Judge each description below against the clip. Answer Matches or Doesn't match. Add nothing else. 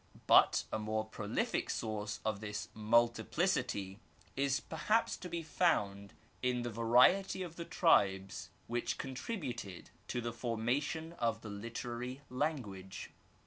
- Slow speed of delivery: Matches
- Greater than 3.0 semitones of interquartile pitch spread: Matches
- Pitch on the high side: Doesn't match